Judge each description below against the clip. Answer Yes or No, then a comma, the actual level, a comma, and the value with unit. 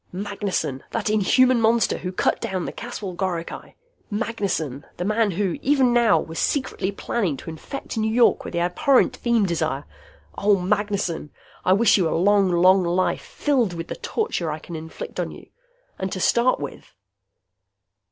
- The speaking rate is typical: Yes, average, 165 wpm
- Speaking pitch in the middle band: No, high, 195 Hz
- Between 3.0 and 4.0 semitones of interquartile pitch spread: No, average, 4.8 semitones